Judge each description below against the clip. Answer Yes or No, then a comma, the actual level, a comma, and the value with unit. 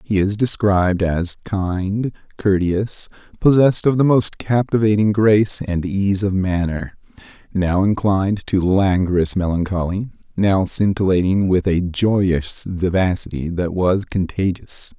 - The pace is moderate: No, slow, 120 wpm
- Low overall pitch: Yes, very low, 95 Hz